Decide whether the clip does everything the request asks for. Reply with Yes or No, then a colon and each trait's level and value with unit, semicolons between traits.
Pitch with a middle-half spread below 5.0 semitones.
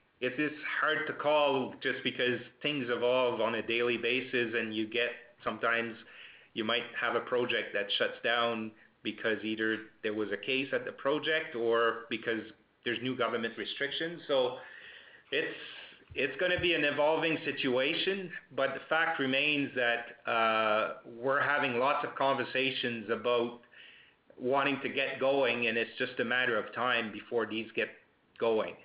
Yes: average, 3.5 semitones